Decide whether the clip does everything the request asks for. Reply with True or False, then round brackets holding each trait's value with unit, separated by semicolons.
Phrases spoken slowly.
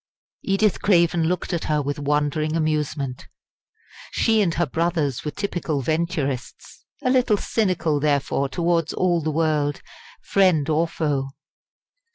True (130 wpm)